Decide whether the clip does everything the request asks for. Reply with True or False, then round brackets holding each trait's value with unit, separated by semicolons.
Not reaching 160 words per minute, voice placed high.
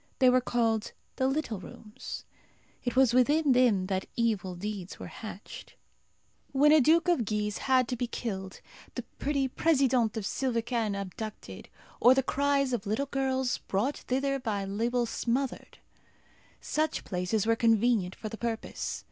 True (150 wpm; 235 Hz)